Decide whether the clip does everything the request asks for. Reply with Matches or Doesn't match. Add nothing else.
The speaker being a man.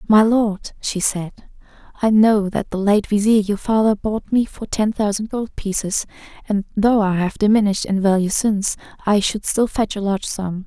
Doesn't match